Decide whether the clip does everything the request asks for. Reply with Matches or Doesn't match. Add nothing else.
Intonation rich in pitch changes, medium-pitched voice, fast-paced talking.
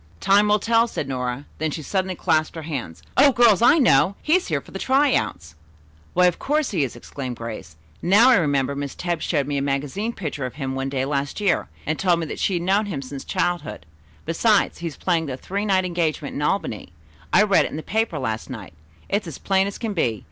Matches